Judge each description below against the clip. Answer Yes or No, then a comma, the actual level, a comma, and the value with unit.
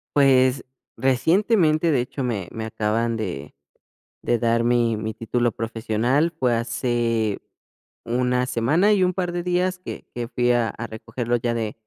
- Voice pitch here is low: Yes, low, 120 Hz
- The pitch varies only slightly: No, average, 3.3 semitones